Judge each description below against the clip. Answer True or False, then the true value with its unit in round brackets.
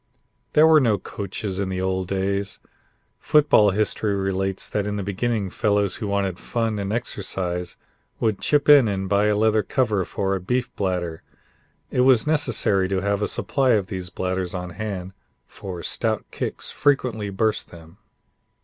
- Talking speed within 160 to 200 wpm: True (165 wpm)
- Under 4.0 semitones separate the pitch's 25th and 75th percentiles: True (2.8 semitones)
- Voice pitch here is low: True (100 Hz)